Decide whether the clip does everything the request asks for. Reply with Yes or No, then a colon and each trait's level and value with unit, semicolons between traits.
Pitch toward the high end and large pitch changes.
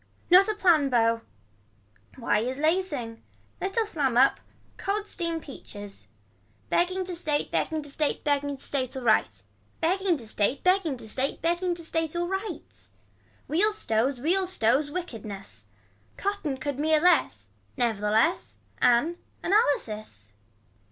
Yes: very high, 295 Hz; wide, 6.8 semitones